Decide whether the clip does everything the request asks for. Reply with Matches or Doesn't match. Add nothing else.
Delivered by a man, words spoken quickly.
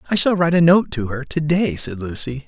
Matches